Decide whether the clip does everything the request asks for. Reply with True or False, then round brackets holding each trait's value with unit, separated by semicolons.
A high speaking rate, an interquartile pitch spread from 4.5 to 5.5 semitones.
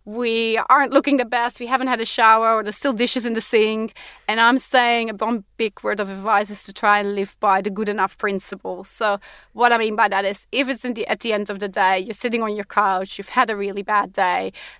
False (260 wpm; 2.9 semitones)